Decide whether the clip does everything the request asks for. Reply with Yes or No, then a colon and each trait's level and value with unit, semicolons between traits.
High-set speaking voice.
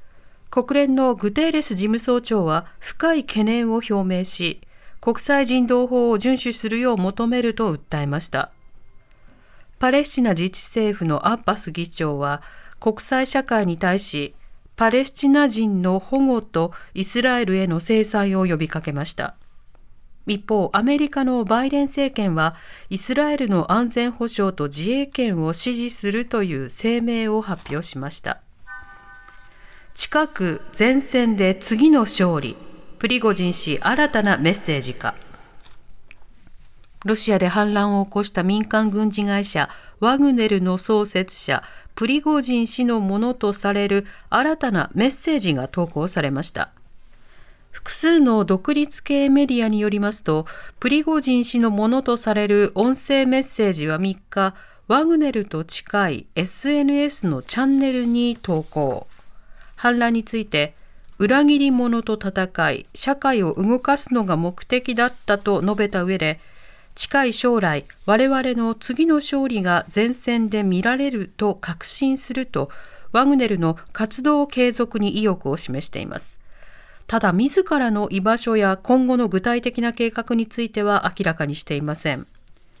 Yes: high, 220 Hz